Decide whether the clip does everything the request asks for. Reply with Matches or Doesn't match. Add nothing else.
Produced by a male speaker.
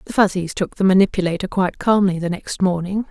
Doesn't match